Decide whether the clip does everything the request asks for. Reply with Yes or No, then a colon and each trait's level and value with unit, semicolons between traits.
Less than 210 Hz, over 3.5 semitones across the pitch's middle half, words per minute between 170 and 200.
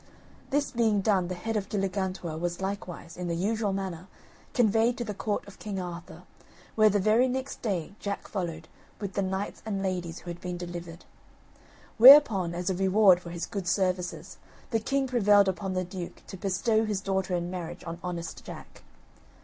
No: high, 190 Hz; average, 3.1 semitones; average, 180 wpm